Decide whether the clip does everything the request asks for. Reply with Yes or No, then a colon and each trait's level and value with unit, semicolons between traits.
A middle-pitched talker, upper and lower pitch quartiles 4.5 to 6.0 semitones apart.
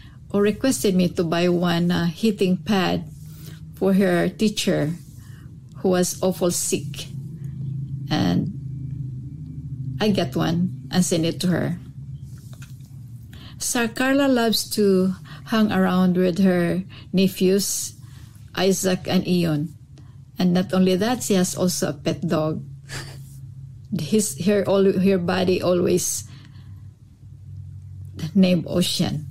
Yes: medium, 165 Hz; wide, 5.6 semitones